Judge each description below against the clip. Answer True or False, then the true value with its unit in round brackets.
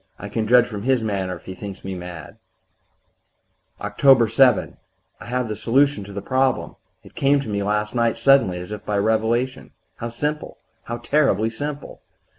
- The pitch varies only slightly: False (4.1 semitones)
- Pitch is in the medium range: False (115 Hz)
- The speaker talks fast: False (170 wpm)